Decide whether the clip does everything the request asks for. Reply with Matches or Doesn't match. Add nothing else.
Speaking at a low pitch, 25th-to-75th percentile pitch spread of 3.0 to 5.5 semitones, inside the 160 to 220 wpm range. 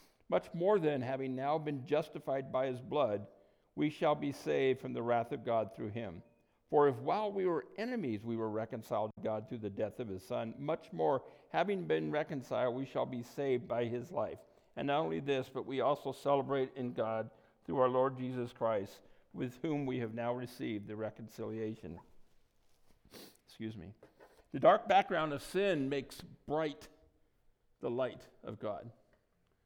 Matches